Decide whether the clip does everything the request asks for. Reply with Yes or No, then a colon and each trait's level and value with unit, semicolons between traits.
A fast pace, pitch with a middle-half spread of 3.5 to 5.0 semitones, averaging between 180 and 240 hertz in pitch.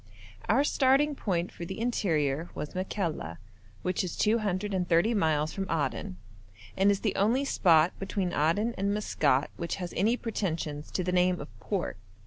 No: average, 155 wpm; average, 4.2 semitones; medium, 185 Hz